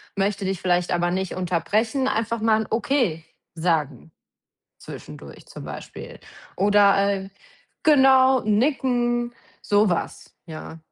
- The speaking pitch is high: Yes, high, 205 Hz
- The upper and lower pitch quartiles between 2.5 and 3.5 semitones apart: No, average, 5.2 semitones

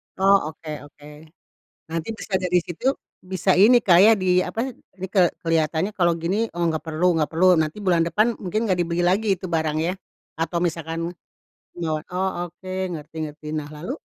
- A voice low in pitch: No, medium, 170 Hz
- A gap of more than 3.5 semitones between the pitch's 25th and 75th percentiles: No, average, 2.9 semitones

